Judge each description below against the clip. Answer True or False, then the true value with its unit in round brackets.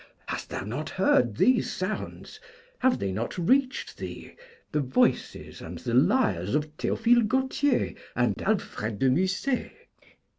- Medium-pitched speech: True (165 Hz)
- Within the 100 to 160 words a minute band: True (135 wpm)